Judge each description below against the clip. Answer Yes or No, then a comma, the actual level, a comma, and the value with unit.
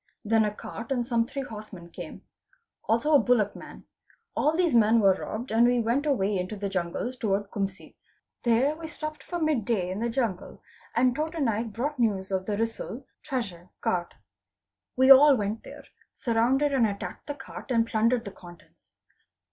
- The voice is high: Yes, high, 230 Hz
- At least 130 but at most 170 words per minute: No, average, 180 wpm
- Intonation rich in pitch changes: No, average, 4.6 semitones